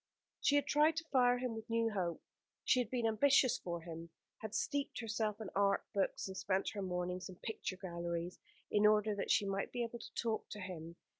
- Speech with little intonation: No, average, 4.3 semitones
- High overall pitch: Yes, high, 210 Hz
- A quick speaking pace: Yes, fast, 210 wpm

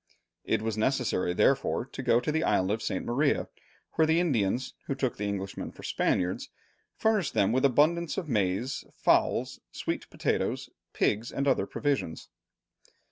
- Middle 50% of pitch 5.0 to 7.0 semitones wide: Yes, wide, 5.5 semitones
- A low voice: Yes, low, 130 Hz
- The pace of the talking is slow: No, average, 155 wpm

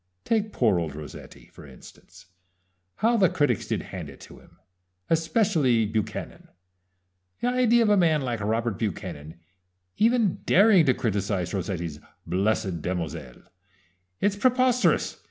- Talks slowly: Yes, slow, 130 wpm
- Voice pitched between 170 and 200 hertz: No, low, 120 Hz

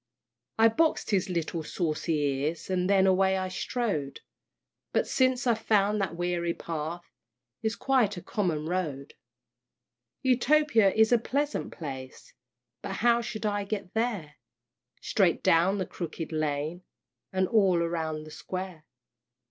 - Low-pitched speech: No, medium, 185 Hz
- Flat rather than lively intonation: No, average, 5.1 semitones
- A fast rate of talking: No, slow, 135 wpm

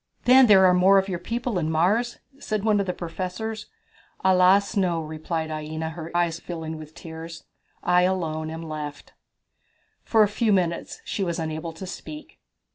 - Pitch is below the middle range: No, medium, 175 Hz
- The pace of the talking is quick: No, average, 170 wpm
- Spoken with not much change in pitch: No, average, 3.5 semitones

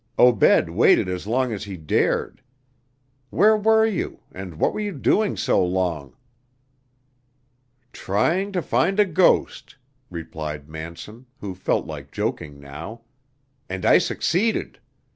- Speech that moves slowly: Yes, slow, 125 wpm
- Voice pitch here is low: Yes, low, 105 Hz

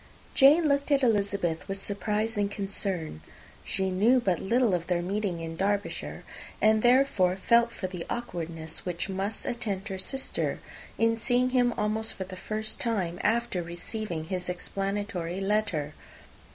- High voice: Yes, high, 200 Hz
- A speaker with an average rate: Yes, average, 150 wpm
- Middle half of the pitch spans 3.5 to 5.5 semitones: Yes, average, 3.9 semitones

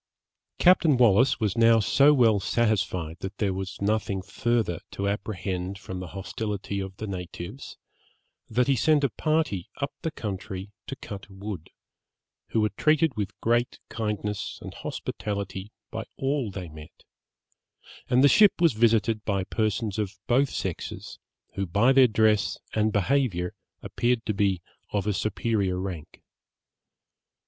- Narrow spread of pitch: No, average, 3.7 semitones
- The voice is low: Yes, low, 105 Hz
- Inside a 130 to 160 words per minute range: Yes, average, 145 wpm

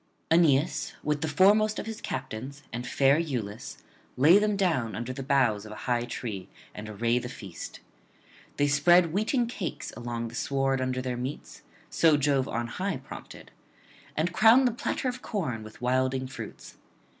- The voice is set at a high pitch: No, low, 135 Hz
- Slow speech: No, average, 165 wpm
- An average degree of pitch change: No, wide, 6.1 semitones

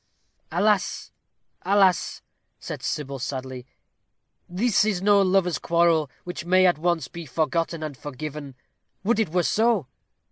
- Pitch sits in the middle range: Yes, medium, 170 Hz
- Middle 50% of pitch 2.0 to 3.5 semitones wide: No, average, 4.2 semitones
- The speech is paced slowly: Yes, slow, 130 wpm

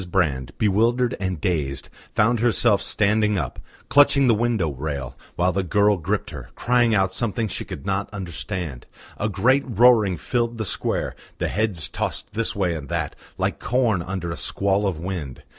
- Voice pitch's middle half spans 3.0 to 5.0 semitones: Yes, average, 4.7 semitones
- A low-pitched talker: Yes, low, 100 Hz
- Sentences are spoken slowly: No, average, 170 wpm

